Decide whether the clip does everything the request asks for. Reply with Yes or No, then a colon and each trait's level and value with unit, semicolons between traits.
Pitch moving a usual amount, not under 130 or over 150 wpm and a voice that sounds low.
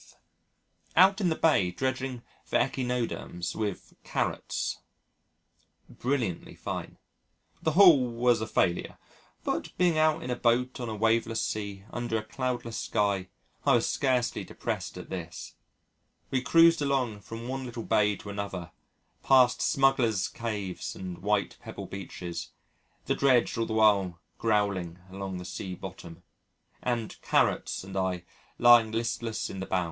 Yes: average, 4.6 semitones; average, 140 wpm; low, 115 Hz